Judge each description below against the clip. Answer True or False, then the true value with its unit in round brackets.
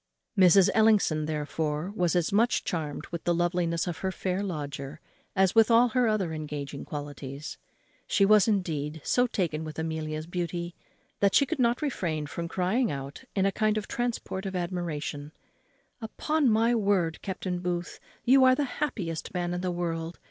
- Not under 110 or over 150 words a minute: False (170 wpm)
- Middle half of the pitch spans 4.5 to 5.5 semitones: True (5.1 semitones)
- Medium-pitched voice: True (175 Hz)